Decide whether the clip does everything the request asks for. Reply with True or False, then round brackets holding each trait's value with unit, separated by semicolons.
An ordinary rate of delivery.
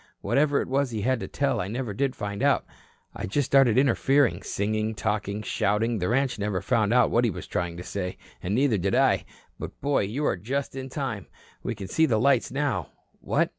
False (210 wpm)